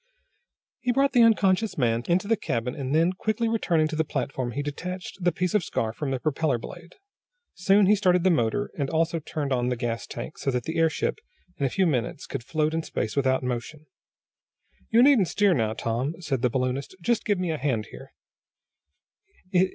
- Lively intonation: Yes, wide, 6.2 semitones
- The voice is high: No, medium, 155 Hz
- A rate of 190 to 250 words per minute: Yes, average, 195 wpm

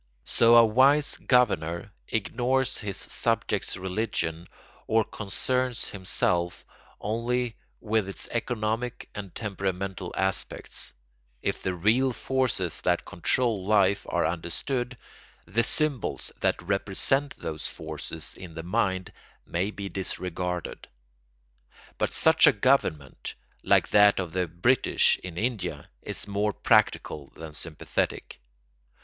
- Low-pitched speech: Yes, low, 100 Hz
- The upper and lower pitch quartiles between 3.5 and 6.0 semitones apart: Yes, average, 4.7 semitones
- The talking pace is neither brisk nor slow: No, slow, 115 wpm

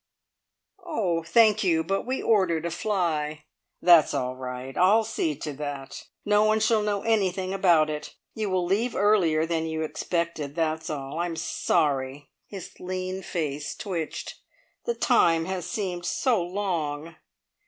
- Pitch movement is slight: No, average, 4.3 semitones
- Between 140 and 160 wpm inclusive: Yes, average, 145 wpm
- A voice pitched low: No, medium, 175 Hz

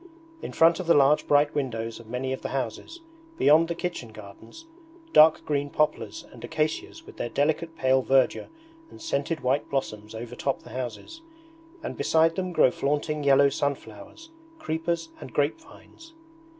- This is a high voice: No, medium, 145 Hz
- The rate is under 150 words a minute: No, average, 160 wpm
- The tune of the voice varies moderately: Yes, average, 4.1 semitones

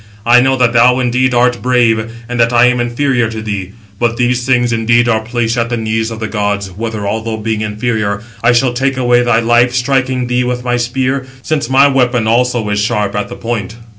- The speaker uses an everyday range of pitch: No, narrow, 1.9 semitones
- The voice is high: No, low, 120 Hz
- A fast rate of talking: Yes, fast, 215 wpm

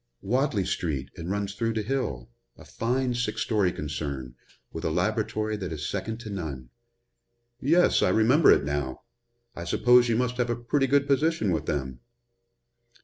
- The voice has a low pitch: Yes, low, 105 Hz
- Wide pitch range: Yes, wide, 8.1 semitones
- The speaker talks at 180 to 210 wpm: No, average, 165 wpm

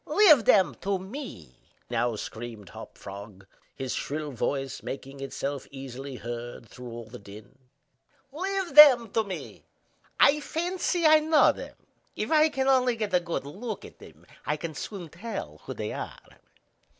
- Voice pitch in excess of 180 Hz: No, medium, 170 Hz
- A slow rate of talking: No, average, 160 wpm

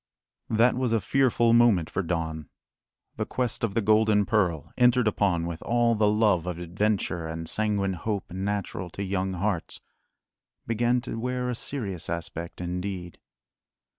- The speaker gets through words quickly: No, average, 150 wpm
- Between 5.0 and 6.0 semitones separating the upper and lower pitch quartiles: No, average, 4.6 semitones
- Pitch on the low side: Yes, low, 100 Hz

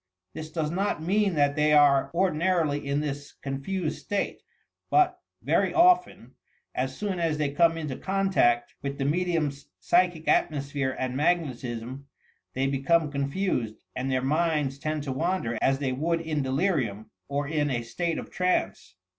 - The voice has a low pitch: No, medium, 150 Hz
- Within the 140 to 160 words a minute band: Yes, average, 155 wpm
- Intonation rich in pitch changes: No, average, 4.0 semitones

